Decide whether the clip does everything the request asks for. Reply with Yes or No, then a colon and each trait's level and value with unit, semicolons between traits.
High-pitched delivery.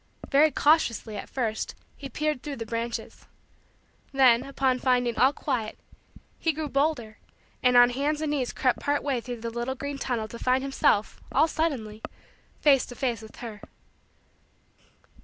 Yes: very high, 255 Hz